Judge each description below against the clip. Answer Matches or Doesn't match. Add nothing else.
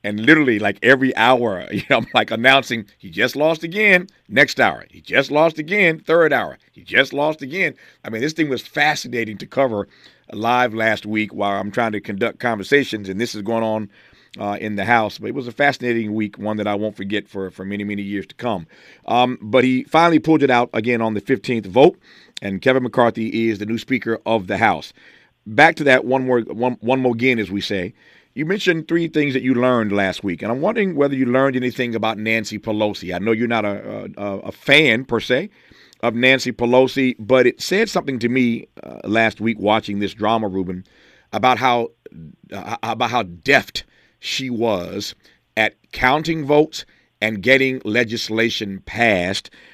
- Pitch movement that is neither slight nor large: Matches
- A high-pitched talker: Doesn't match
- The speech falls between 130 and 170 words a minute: Doesn't match